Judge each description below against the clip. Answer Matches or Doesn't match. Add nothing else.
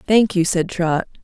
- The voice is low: Doesn't match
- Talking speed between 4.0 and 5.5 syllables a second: Matches